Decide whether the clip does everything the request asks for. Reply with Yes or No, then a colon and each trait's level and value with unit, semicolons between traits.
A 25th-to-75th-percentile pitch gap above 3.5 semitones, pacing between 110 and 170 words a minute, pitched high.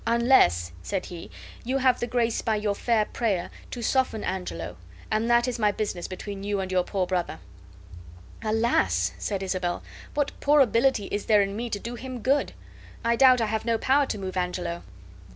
No: average, 4.2 semitones; average, 190 wpm; high, 215 Hz